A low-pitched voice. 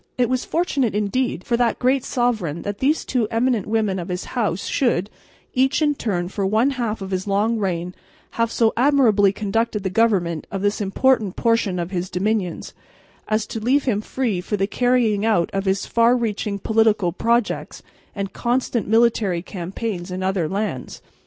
No: high, 215 Hz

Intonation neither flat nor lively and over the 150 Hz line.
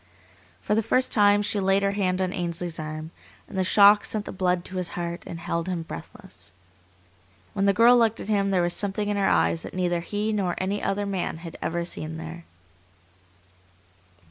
Yes: average, 3.0 semitones; medium, 185 Hz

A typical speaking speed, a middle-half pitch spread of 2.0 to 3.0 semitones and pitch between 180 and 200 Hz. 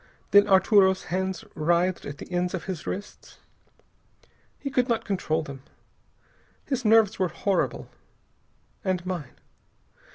No: slow, 125 wpm; average, 2.7 semitones; high, 190 Hz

